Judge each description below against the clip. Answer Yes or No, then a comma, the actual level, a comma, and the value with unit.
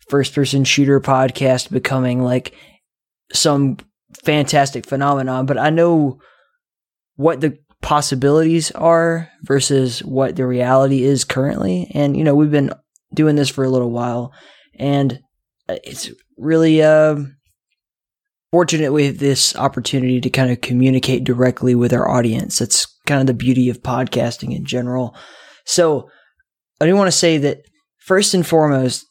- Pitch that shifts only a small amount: No, average, 3.3 semitones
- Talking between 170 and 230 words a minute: No, average, 140 wpm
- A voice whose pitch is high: No, medium, 140 Hz